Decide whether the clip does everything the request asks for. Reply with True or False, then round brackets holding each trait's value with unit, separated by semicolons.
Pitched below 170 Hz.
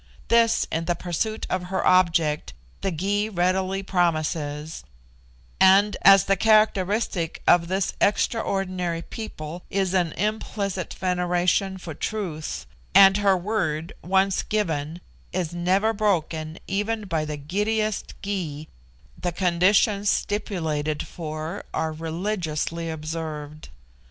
False (180 Hz)